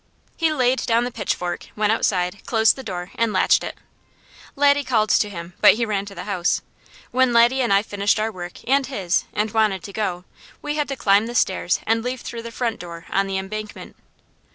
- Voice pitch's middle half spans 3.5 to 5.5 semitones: Yes, average, 3.8 semitones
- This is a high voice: Yes, high, 215 Hz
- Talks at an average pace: No, fast, 210 wpm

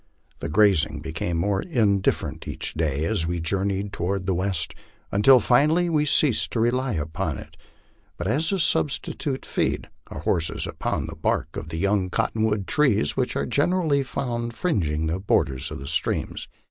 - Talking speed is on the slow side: No, average, 175 wpm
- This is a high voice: No, low, 100 Hz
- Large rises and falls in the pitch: Yes, wide, 8.0 semitones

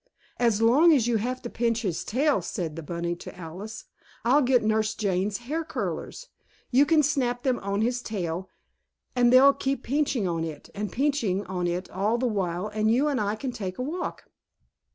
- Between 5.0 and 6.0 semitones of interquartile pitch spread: Yes, average, 5.3 semitones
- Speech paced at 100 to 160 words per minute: No, average, 195 wpm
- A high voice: Yes, high, 225 Hz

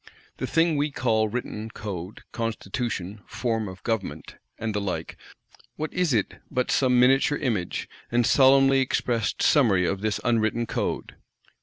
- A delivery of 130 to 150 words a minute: Yes, average, 145 wpm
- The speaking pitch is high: No, low, 115 Hz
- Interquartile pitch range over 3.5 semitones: Yes, average, 3.9 semitones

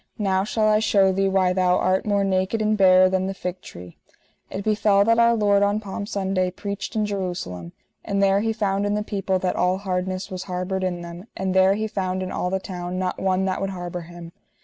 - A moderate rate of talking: No, fast, 225 wpm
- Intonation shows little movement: Yes, narrow, 1.6 semitones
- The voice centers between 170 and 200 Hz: Yes, high, 190 Hz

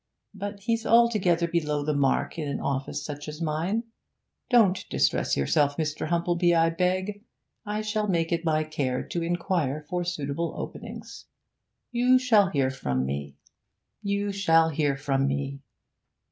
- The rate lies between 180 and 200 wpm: No, average, 145 wpm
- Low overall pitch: No, medium, 165 Hz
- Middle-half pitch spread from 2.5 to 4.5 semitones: No, wide, 5.6 semitones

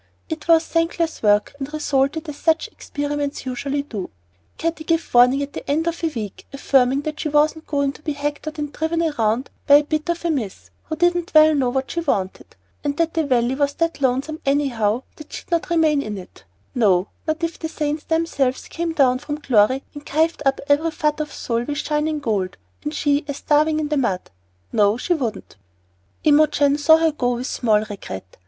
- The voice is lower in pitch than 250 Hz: No, very high, 290 Hz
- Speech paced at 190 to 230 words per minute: Yes, average, 200 wpm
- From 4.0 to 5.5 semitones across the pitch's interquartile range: No, average, 3.6 semitones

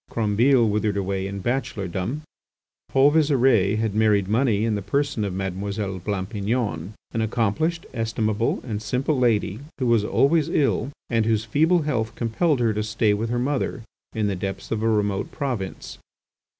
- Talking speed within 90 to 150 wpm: No, average, 160 wpm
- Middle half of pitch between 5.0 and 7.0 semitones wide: No, average, 3.9 semitones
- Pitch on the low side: Yes, low, 110 Hz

